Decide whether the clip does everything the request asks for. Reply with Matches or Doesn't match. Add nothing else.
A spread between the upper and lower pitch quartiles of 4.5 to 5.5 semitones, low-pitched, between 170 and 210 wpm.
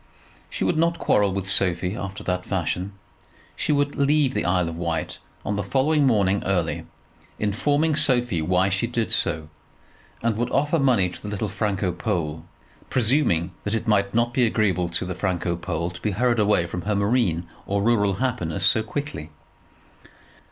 Matches